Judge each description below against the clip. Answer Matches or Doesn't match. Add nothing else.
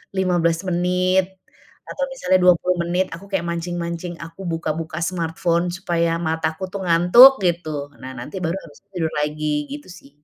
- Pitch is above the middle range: Doesn't match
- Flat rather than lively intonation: Matches